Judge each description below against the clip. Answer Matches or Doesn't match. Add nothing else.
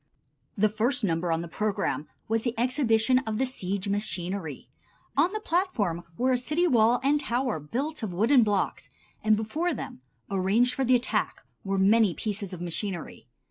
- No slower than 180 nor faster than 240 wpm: Doesn't match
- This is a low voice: Doesn't match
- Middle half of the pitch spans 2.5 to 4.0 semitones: Doesn't match